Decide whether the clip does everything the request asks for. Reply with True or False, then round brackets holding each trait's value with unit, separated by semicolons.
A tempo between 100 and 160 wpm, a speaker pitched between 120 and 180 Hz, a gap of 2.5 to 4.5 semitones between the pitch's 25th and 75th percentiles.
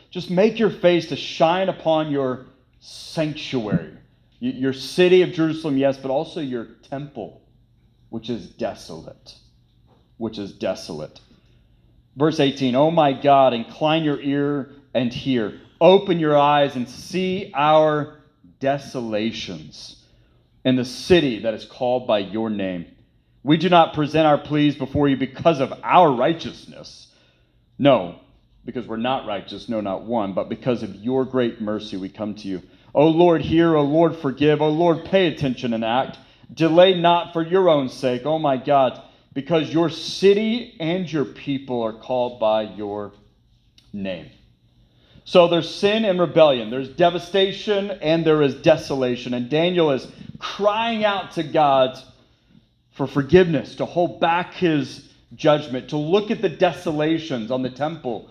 False (155 wpm; 140 Hz; 5.2 semitones)